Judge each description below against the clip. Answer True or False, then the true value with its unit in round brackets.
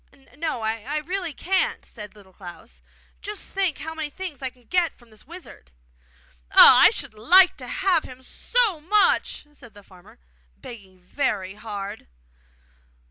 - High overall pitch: True (260 Hz)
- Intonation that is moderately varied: False (8.9 semitones)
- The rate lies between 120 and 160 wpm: True (150 wpm)